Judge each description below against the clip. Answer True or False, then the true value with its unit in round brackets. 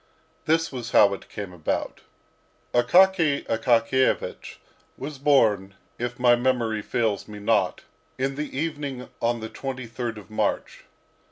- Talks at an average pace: False (125 wpm)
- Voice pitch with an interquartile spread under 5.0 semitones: True (3.6 semitones)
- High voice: False (120 Hz)